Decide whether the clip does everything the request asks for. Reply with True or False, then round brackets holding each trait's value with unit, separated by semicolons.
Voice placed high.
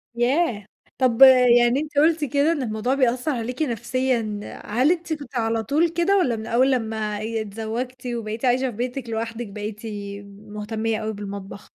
True (240 Hz)